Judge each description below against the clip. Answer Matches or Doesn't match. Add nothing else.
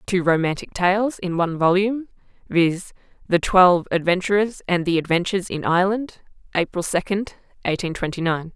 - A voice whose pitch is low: Doesn't match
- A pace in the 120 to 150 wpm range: Matches